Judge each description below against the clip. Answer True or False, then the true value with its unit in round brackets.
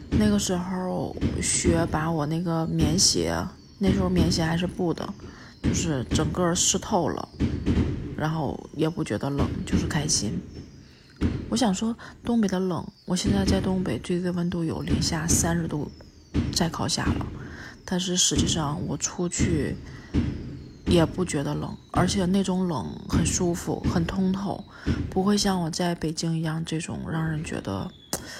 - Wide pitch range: False (2.6 semitones)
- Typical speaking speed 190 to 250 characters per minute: True (220 characters per minute)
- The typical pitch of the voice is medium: True (170 Hz)